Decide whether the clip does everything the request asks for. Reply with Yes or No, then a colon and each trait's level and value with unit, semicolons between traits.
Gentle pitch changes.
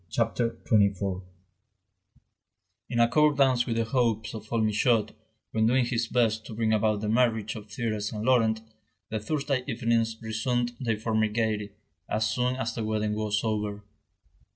Yes: narrow, 1.9 semitones